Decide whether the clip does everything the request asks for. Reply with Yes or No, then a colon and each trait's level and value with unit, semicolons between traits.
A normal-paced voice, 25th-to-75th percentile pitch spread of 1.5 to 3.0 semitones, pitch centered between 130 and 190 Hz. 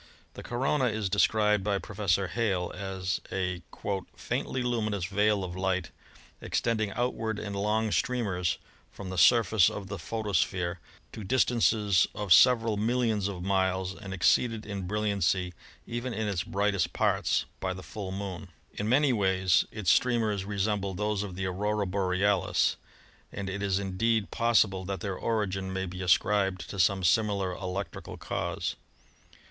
No: average, 150 wpm; narrow, 2.4 semitones; low, 100 Hz